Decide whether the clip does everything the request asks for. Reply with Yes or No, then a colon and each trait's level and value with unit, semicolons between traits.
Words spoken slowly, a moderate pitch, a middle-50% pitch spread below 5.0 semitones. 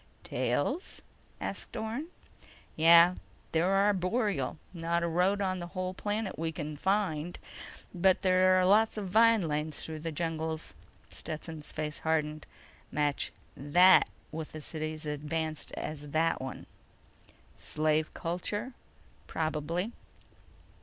Yes: slow, 125 wpm; medium, 165 Hz; average, 3.3 semitones